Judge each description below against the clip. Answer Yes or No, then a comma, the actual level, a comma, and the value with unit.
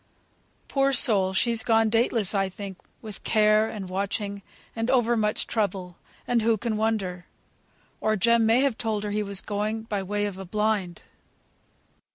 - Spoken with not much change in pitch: Yes, narrow, 2.3 semitones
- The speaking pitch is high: Yes, high, 215 Hz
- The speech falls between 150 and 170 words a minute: Yes, average, 165 wpm